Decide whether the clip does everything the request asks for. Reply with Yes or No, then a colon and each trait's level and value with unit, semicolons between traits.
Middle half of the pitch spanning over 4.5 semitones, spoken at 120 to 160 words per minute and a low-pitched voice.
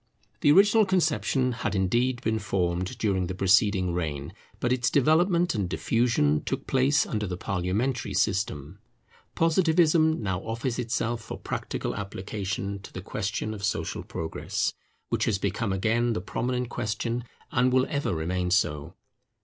Yes: average, 5.3 semitones; average, 145 wpm; low, 110 Hz